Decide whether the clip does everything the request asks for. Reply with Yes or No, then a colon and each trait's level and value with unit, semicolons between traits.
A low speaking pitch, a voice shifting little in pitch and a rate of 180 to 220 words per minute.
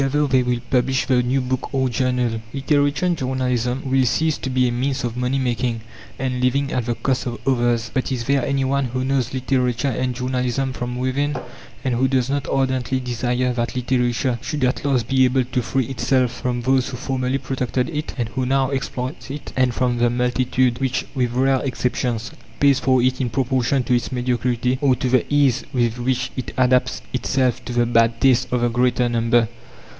Yes: low, 125 Hz; narrow, 1.5 semitones; average, 200 wpm